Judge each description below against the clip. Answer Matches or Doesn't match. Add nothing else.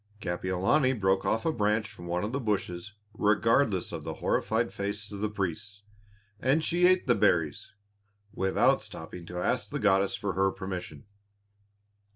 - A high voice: Doesn't match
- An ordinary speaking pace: Matches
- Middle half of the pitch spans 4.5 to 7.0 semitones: Doesn't match